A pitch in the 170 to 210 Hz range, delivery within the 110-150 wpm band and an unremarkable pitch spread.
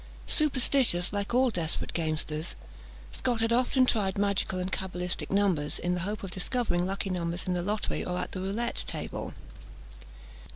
No: high, 190 Hz; average, 160 wpm; average, 4.1 semitones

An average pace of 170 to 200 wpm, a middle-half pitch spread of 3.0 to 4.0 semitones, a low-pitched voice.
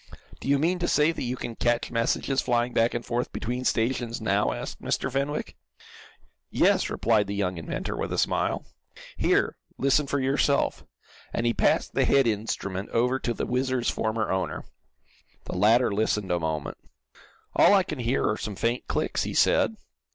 Yes: average, 175 wpm; average, 3.6 semitones; low, 120 Hz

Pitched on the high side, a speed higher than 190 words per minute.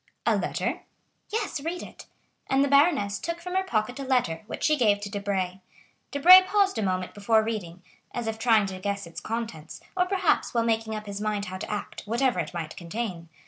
Yes: high, 220 Hz; fast, 205 wpm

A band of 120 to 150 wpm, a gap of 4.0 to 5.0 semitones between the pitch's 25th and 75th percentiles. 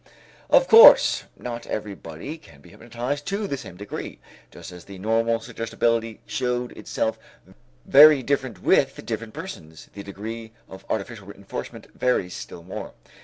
Yes: average, 140 wpm; average, 4.3 semitones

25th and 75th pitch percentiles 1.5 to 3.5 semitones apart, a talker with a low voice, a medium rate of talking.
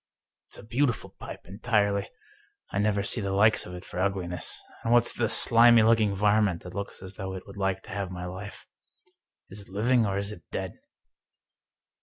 Yes: narrow, 2.4 semitones; low, 100 Hz; average, 190 wpm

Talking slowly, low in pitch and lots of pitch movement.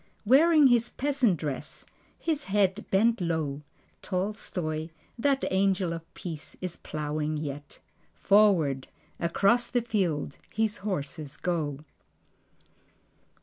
No: slow, 105 wpm; medium, 185 Hz; wide, 6.1 semitones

